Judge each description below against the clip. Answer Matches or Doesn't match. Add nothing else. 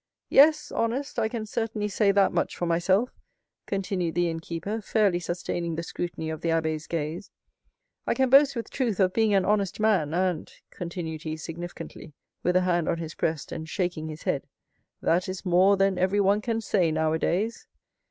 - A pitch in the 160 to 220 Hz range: Matches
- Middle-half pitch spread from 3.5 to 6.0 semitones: Matches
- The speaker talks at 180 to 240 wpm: Doesn't match